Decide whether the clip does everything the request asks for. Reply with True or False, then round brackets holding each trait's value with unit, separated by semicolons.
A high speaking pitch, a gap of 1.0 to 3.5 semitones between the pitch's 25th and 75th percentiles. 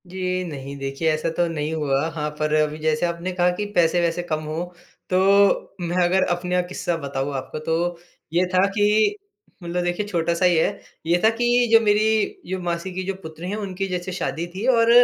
False (175 Hz; 2.9 semitones)